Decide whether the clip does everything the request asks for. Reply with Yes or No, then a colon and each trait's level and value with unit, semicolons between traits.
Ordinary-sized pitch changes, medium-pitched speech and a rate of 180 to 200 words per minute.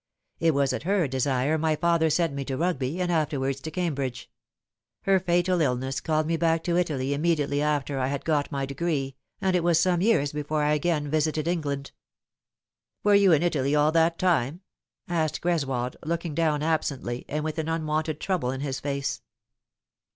Yes: average, 3.3 semitones; medium, 155 Hz; average, 185 wpm